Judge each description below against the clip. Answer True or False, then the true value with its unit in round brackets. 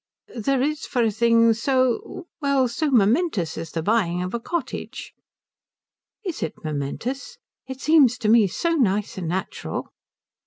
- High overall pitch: True (235 Hz)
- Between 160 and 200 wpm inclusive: False (150 wpm)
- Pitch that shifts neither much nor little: False (5.9 semitones)